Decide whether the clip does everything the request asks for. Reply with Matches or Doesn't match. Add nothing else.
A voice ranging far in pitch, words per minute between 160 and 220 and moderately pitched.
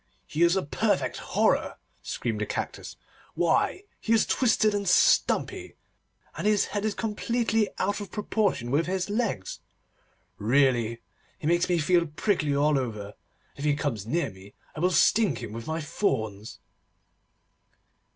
Doesn't match